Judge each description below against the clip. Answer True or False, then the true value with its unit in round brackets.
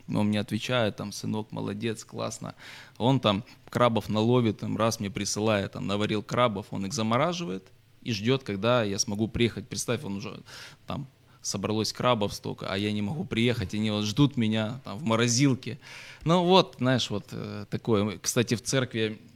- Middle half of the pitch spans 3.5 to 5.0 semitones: False (3.0 semitones)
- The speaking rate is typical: False (175 wpm)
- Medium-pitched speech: False (110 Hz)